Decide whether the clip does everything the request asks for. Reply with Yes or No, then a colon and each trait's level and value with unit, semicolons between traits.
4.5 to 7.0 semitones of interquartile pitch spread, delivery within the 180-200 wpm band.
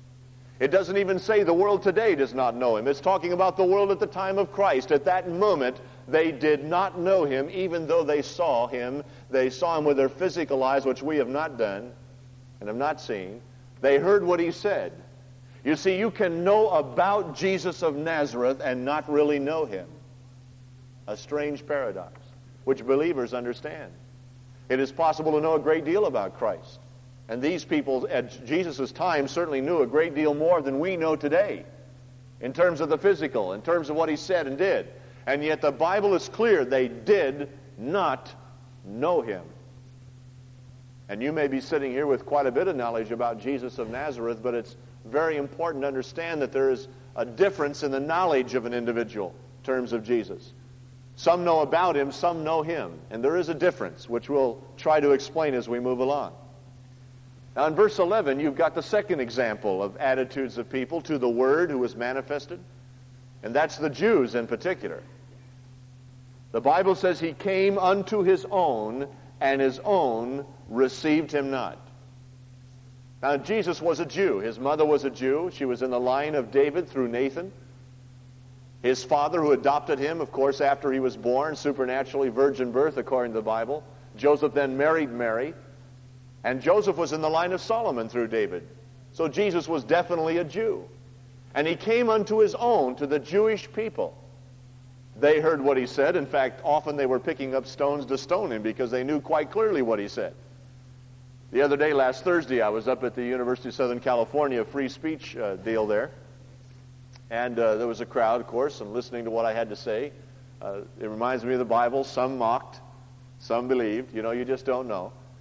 No: average, 3.7 semitones; average, 190 wpm